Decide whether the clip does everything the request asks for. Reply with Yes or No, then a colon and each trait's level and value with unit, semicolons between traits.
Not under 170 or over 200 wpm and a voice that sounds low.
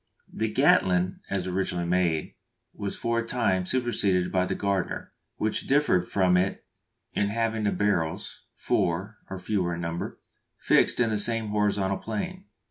No: average, 155 wpm; low, 100 Hz